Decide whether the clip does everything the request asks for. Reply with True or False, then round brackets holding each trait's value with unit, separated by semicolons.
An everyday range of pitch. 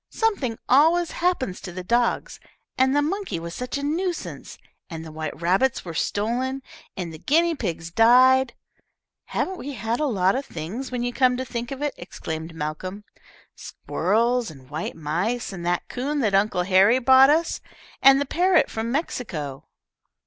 False (7.2 semitones)